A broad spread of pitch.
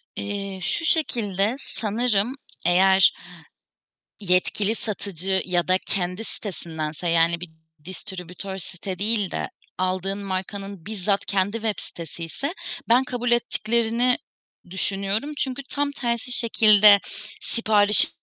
No: average, 3.5 semitones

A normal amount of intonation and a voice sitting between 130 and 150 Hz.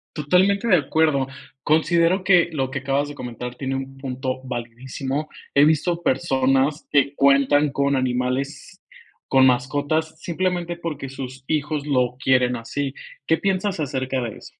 Yes: average, 3.2 semitones; medium, 140 Hz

